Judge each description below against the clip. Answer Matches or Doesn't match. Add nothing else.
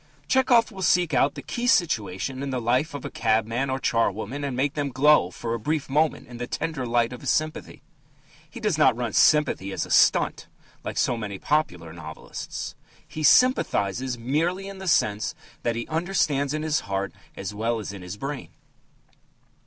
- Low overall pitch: Matches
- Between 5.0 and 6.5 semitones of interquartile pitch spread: Matches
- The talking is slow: Doesn't match